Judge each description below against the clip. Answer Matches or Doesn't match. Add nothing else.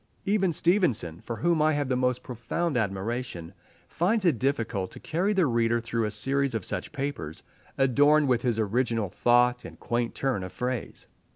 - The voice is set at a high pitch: Doesn't match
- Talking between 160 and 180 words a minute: Matches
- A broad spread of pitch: Doesn't match